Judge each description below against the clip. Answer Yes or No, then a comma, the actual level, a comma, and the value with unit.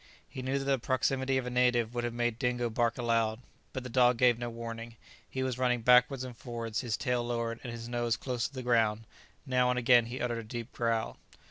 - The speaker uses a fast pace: Yes, fast, 230 wpm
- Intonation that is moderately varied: No, narrow, 1.4 semitones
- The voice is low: Yes, low, 120 Hz